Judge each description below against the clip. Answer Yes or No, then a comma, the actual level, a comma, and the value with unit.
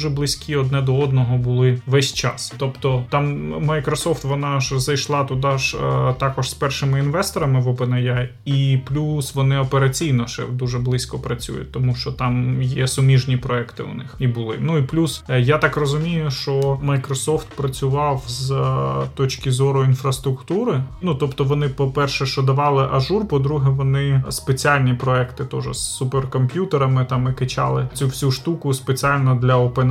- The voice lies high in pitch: No, low, 135 Hz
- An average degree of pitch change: No, narrow, 1.9 semitones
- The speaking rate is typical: No, fast, 160 wpm